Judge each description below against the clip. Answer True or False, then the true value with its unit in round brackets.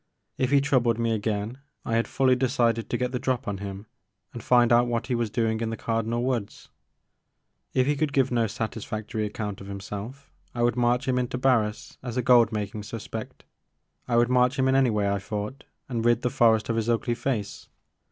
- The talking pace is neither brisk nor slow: False (210 wpm)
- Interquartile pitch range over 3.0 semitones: False (2.6 semitones)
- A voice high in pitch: False (120 Hz)